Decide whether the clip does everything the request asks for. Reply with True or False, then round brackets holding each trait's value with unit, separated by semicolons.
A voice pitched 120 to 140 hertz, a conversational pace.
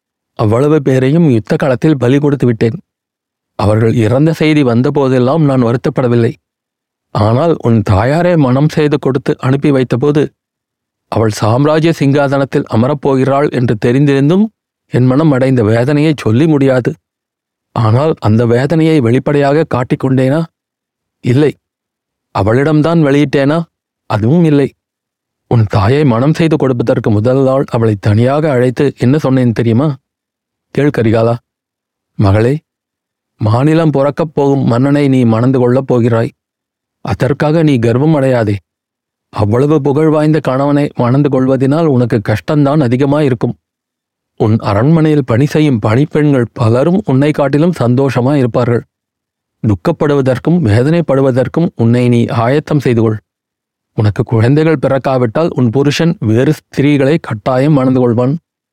True (135 Hz; 110 wpm)